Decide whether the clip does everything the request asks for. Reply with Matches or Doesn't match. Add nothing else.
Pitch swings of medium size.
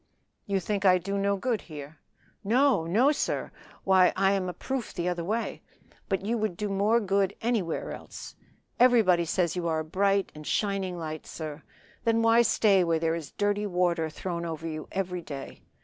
Matches